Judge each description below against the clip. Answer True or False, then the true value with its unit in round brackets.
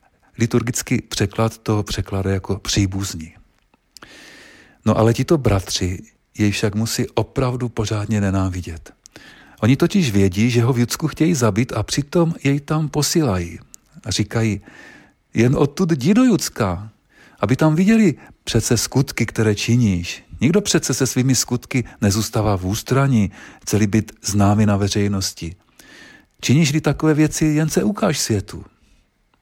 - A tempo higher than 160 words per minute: False (130 wpm)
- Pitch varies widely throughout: True (5.9 semitones)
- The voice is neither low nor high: False (115 Hz)